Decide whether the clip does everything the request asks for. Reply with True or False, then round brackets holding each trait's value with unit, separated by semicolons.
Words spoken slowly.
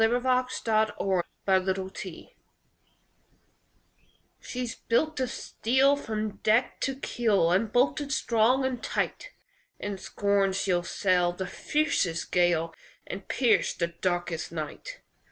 True (120 wpm)